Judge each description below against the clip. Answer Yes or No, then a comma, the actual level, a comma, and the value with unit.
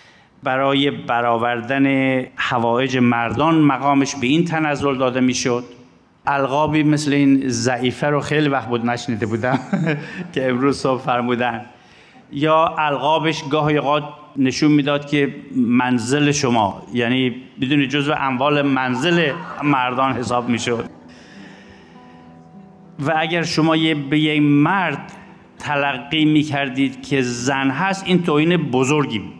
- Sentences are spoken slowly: No, average, 120 wpm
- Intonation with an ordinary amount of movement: Yes, average, 3.3 semitones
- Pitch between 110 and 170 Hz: Yes, medium, 140 Hz